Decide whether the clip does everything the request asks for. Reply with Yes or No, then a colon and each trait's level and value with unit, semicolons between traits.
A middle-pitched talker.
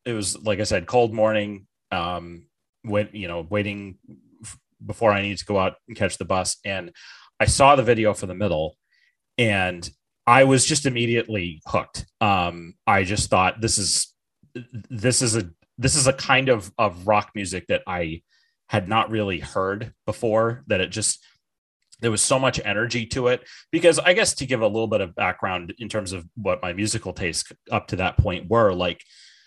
No: low, 105 Hz